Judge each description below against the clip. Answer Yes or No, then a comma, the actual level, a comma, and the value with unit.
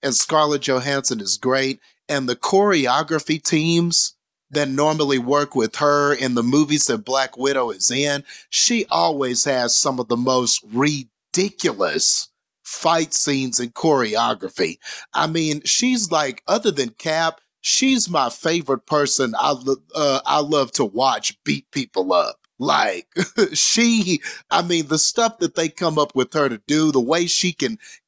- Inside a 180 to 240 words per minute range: No, average, 155 wpm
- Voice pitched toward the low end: No, medium, 150 Hz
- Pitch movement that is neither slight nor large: Yes, average, 3.8 semitones